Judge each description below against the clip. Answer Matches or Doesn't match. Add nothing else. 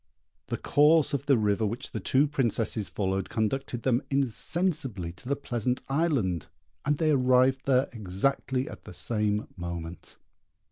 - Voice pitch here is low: Matches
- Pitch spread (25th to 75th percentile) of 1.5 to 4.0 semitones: Doesn't match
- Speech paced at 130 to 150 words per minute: Matches